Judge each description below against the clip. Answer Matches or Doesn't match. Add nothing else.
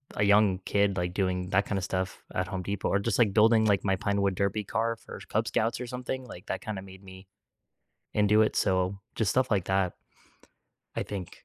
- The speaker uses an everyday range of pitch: Doesn't match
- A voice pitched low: Matches